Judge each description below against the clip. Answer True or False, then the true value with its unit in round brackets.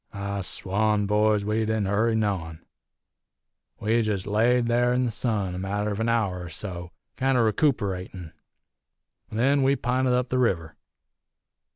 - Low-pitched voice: True (105 Hz)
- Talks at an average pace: True (145 wpm)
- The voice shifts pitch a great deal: False (3.4 semitones)